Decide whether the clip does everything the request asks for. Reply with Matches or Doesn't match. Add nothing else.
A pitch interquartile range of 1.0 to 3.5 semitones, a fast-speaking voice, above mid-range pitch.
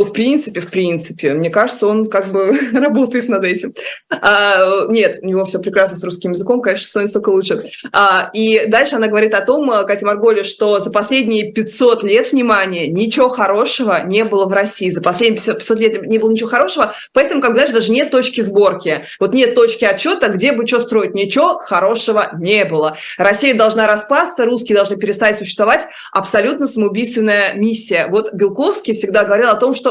Matches